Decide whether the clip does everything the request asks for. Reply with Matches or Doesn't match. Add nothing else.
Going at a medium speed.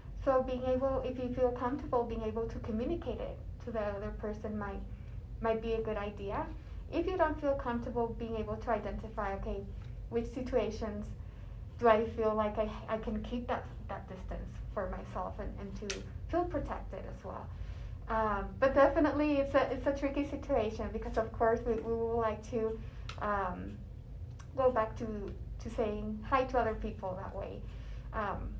Matches